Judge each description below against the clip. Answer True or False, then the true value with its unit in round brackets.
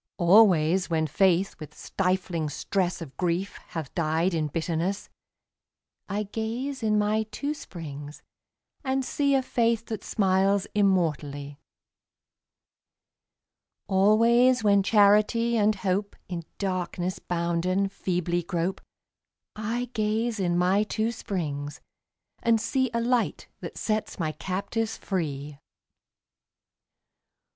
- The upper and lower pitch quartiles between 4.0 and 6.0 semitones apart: True (4.4 semitones)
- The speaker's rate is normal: False (110 wpm)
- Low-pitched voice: False (195 Hz)